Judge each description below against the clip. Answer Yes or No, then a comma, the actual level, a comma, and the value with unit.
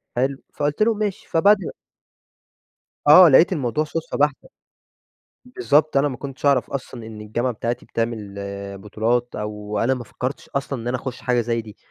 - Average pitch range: Yes, average, 4.1 semitones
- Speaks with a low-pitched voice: Yes, low, 130 Hz